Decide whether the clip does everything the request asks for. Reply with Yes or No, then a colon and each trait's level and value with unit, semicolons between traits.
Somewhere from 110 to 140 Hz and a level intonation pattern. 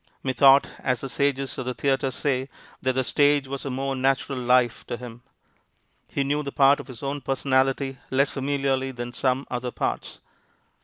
Yes: low, 135 Hz; narrow, 1.4 semitones